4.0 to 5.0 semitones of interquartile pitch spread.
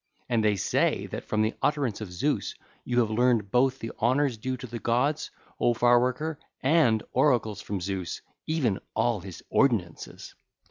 No: average, 3.4 semitones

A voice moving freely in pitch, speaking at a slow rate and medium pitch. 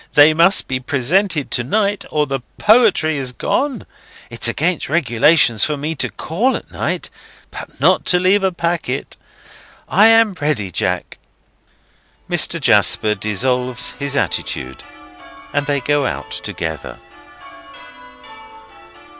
Yes: wide, 6.3 semitones; slow, 125 wpm; medium, 145 Hz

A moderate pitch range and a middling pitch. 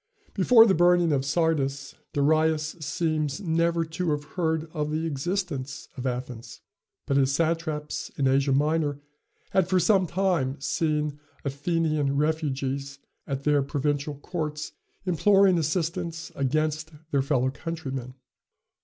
Yes: average, 3.0 semitones; medium, 155 Hz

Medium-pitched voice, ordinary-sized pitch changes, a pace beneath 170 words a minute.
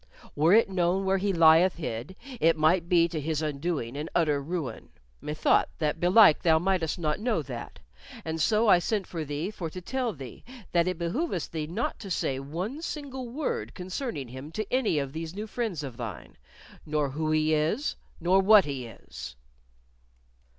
No: medium, 165 Hz; average, 4.2 semitones; average, 180 wpm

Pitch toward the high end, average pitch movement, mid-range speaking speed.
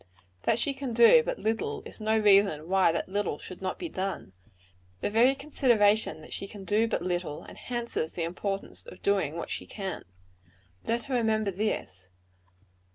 Yes: high, 205 Hz; average, 4.0 semitones; average, 170 wpm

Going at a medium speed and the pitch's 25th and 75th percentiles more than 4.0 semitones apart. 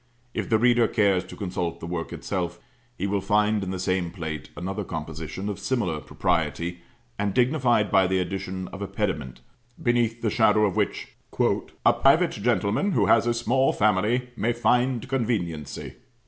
Yes: average, 165 wpm; average, 4.7 semitones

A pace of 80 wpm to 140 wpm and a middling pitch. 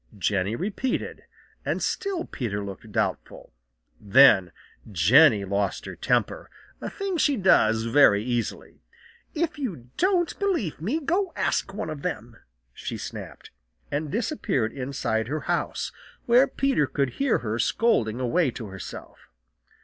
Yes: slow, 135 wpm; medium, 145 Hz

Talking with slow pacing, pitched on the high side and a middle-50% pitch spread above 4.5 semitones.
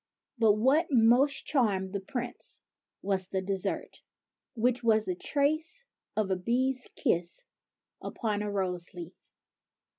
Yes: slow, 125 wpm; high, 215 Hz; average, 5.0 semitones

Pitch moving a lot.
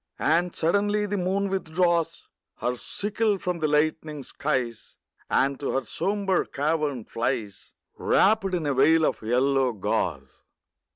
Yes: wide, 5.8 semitones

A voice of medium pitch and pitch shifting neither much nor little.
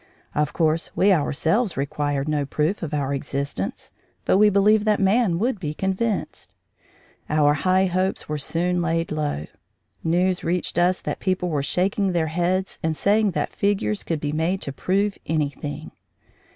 Yes: medium, 175 Hz; average, 4.2 semitones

